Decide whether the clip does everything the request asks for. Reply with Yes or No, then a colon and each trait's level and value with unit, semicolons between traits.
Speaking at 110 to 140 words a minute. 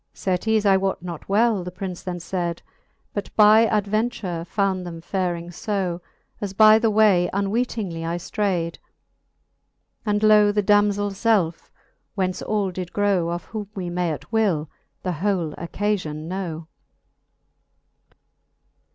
Yes: slow, 135 wpm